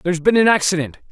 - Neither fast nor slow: No, fast, 215 wpm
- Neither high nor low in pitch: Yes, medium, 180 Hz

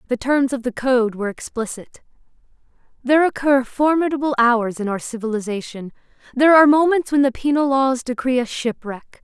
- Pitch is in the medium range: No, very high, 255 Hz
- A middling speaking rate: Yes, average, 155 wpm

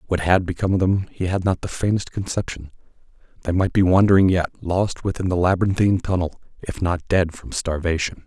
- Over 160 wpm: Yes, average, 180 wpm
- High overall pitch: No, very low, 90 Hz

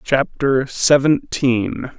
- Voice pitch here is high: No, low, 135 Hz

